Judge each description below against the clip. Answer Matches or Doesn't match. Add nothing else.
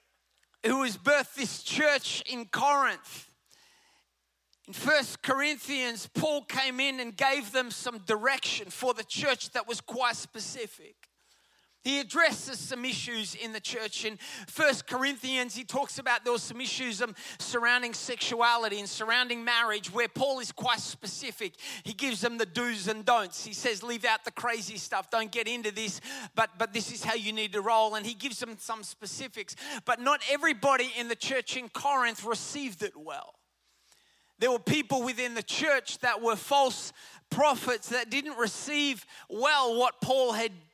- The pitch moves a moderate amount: Matches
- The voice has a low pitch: Doesn't match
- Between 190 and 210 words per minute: Doesn't match